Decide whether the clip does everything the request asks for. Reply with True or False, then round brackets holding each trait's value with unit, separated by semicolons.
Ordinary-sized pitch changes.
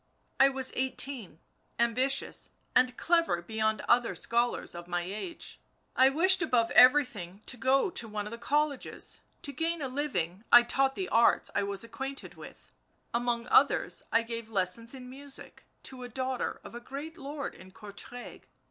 True (3.7 semitones)